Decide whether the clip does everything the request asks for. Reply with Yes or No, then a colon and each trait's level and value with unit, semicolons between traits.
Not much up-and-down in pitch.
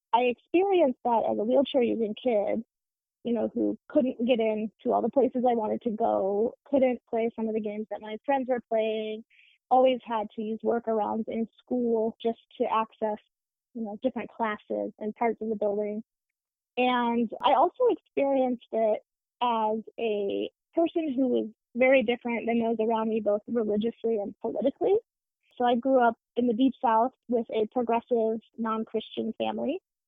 Yes: narrow, 2.3 semitones